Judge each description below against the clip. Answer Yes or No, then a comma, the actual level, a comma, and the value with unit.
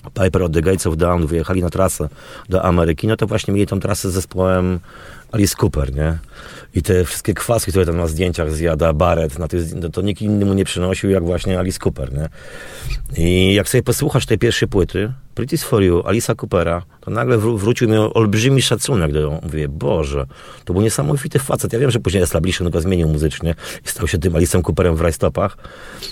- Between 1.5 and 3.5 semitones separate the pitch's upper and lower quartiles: No, average, 4.3 semitones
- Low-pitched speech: Yes, very low, 95 Hz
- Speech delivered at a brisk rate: Yes, fast, 205 wpm